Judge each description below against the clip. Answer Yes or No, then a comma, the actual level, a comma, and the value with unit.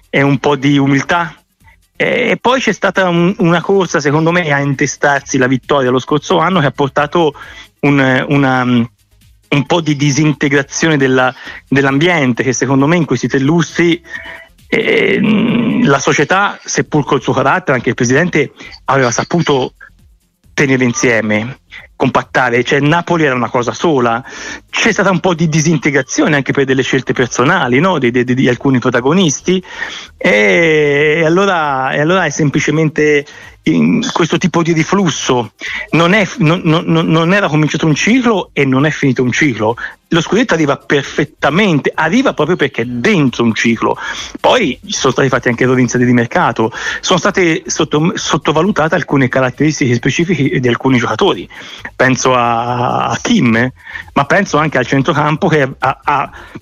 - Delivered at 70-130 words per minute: No, average, 150 wpm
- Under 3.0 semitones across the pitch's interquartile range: No, average, 4.5 semitones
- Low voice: No, medium, 145 Hz